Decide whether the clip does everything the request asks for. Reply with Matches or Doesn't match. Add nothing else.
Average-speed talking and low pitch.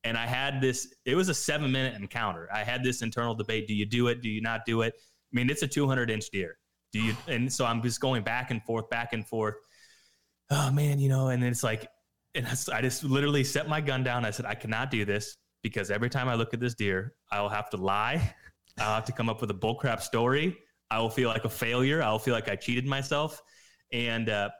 Doesn't match